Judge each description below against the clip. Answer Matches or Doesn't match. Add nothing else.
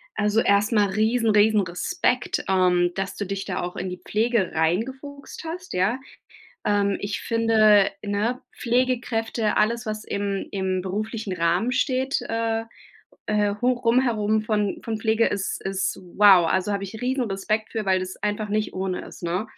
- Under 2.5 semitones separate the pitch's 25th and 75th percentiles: Doesn't match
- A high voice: Matches